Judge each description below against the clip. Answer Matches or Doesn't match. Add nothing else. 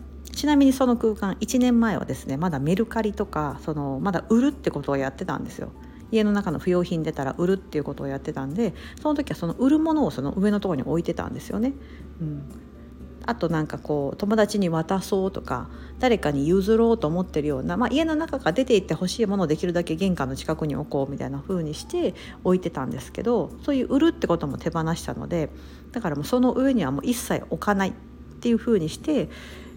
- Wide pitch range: Matches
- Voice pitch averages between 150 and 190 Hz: Matches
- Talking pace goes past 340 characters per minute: Matches